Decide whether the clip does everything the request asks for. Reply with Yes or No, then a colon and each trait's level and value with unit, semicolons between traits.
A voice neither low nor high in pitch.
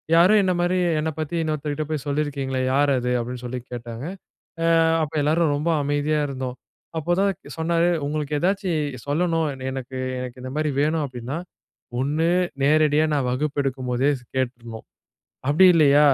Yes: medium, 145 Hz